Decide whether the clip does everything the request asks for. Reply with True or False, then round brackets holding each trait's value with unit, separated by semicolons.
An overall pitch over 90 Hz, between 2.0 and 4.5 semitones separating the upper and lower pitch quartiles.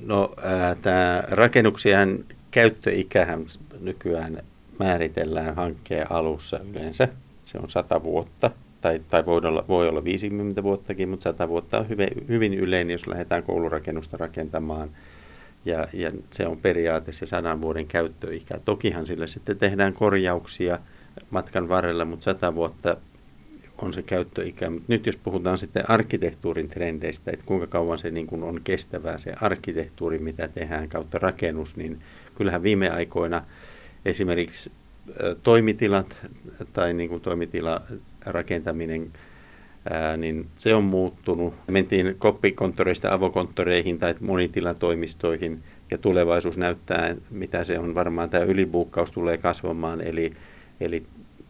False (85 Hz; 2.7 semitones)